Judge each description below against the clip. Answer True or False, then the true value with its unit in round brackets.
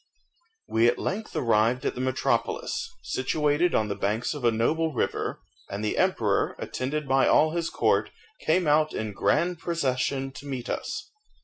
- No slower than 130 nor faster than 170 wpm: True (165 wpm)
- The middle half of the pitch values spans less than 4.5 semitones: False (5.5 semitones)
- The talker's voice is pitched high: False (135 Hz)